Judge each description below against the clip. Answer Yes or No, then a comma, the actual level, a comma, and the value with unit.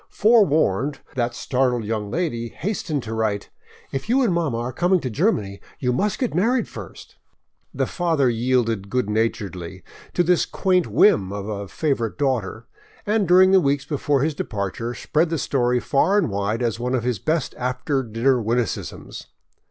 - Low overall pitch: Yes, low, 125 Hz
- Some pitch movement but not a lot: No, wide, 6.6 semitones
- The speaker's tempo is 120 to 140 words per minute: No, average, 165 wpm